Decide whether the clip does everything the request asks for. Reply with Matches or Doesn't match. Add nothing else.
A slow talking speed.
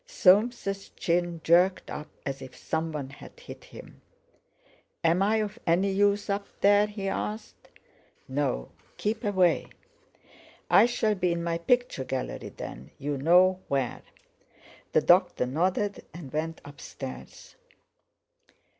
Matches